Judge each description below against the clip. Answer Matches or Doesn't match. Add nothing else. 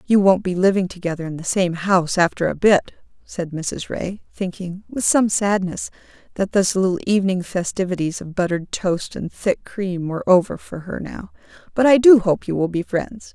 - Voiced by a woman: Matches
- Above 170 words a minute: Matches